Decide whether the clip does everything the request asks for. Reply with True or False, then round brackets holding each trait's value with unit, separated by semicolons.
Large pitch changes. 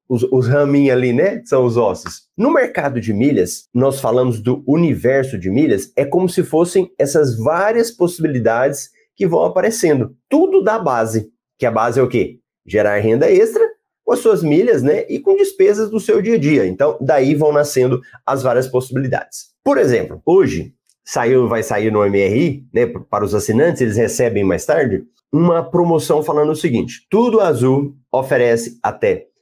True (8.6 semitones)